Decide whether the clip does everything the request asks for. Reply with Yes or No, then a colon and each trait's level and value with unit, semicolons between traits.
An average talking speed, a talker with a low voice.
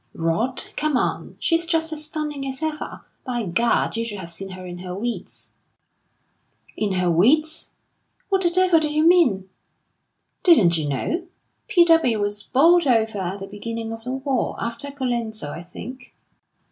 No: average, 165 wpm; high, 240 Hz